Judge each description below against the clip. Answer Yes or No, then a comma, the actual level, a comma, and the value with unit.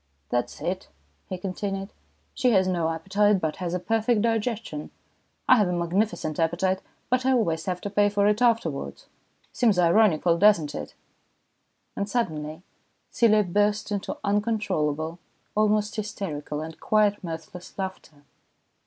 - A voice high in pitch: Yes, high, 195 Hz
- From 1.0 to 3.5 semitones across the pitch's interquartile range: No, average, 4.2 semitones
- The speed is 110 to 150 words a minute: Yes, average, 145 wpm